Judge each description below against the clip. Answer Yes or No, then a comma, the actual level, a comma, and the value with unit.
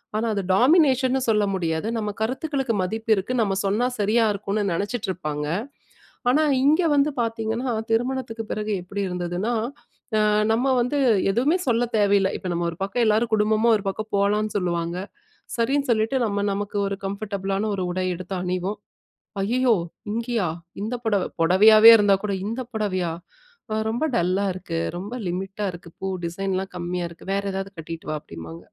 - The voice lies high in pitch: Yes, high, 205 Hz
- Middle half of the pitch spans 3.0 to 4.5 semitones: Yes, average, 3.7 semitones